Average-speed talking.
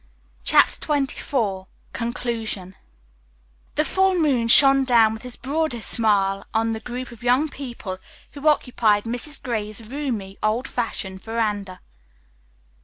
No: slow, 125 wpm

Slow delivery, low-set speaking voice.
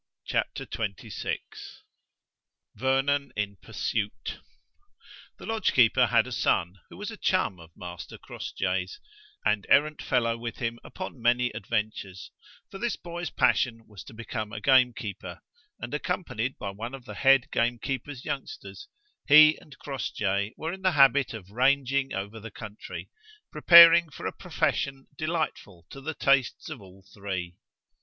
No: average, 145 wpm; low, 125 Hz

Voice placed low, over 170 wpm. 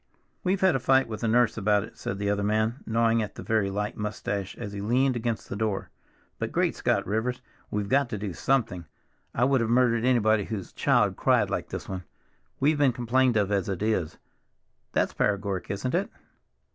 Yes: low, 110 Hz; average, 200 wpm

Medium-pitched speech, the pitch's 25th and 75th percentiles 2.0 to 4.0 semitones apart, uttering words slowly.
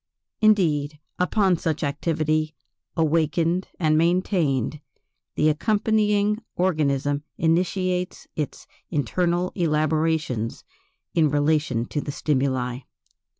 Yes: medium, 155 Hz; average, 3.6 semitones; slow, 85 wpm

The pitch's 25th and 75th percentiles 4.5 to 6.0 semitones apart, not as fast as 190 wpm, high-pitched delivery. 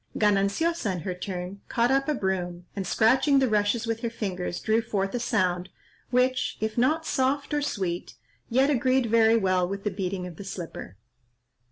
Yes: average, 5.1 semitones; average, 180 wpm; high, 215 Hz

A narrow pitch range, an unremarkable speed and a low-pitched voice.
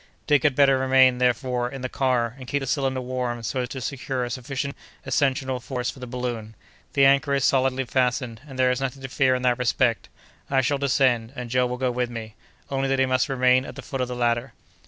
No: narrow, 1.5 semitones; fast, 235 wpm; low, 130 Hz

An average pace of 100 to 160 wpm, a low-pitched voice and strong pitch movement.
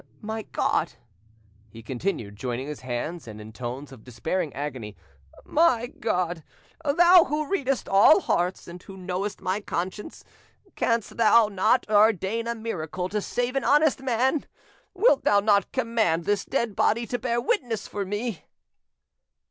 No: average, 145 wpm; high, 205 Hz; wide, 6.8 semitones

